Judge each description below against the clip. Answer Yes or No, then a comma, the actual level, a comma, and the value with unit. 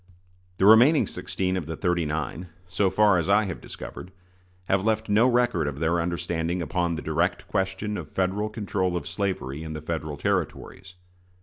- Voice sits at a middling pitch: No, very low, 90 Hz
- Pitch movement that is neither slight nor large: Yes, average, 3.6 semitones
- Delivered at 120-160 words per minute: No, average, 175 wpm